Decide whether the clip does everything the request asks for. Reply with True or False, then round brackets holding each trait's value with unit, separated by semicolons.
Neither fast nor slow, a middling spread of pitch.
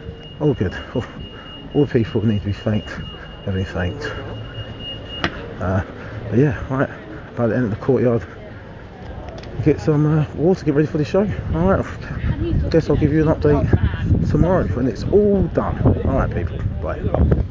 False (170 wpm; 6.1 semitones)